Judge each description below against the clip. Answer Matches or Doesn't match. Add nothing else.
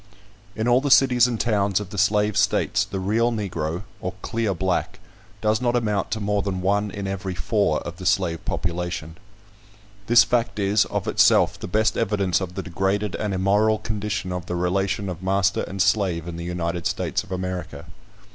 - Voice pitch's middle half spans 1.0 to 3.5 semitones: Matches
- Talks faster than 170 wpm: Matches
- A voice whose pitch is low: Matches